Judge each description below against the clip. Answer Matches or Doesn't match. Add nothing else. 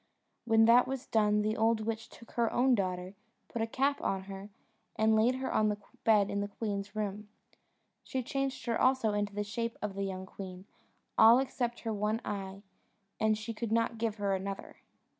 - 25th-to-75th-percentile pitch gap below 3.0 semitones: Matches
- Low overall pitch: Doesn't match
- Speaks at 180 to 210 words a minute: Matches